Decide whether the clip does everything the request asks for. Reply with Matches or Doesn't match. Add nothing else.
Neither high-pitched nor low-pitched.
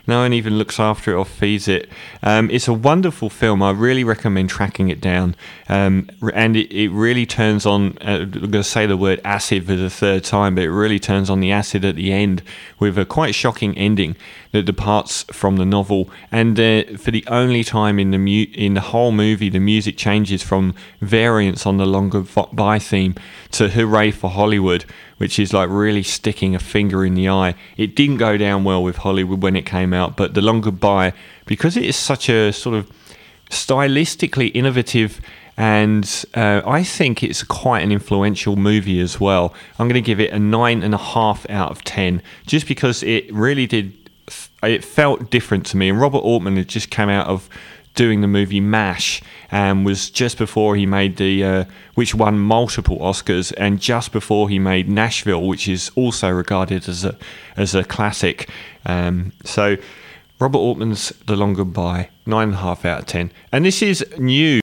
Doesn't match